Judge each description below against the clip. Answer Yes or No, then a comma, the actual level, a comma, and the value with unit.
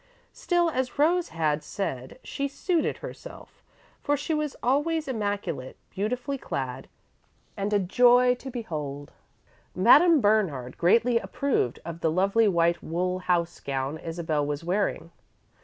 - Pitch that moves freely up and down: Yes, wide, 8.2 semitones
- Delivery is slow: Yes, slow, 130 wpm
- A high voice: Yes, high, 200 Hz